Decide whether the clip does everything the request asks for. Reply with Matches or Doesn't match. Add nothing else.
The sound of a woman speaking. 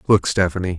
Doesn't match